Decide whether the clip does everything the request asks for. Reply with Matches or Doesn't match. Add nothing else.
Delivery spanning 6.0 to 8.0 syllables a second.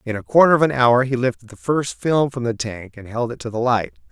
Doesn't match